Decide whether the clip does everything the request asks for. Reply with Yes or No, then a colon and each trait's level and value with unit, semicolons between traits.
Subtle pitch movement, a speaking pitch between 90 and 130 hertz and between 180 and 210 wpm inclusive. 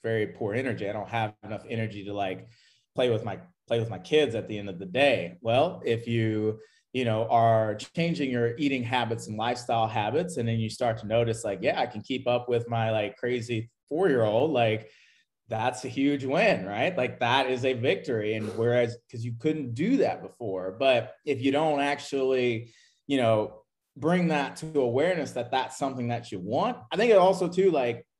No: average, 3.3 semitones; low, 120 Hz; average, 200 wpm